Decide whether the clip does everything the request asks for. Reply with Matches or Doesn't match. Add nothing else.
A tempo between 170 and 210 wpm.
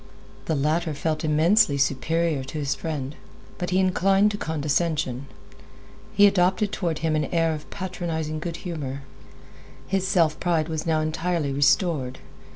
Doesn't match